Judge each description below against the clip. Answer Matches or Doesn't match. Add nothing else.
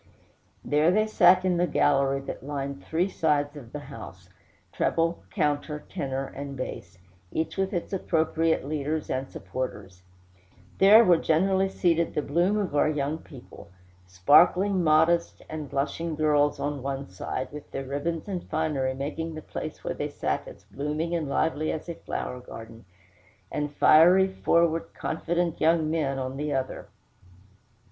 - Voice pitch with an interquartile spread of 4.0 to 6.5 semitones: Doesn't match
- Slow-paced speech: Doesn't match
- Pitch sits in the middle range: Matches